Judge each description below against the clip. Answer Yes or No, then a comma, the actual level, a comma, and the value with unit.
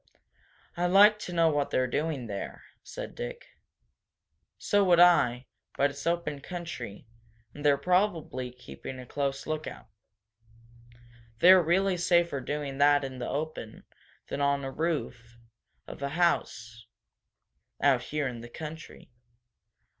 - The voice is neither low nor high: Yes, medium, 145 Hz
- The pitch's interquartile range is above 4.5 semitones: Yes, average, 5.0 semitones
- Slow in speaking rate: Yes, slow, 130 wpm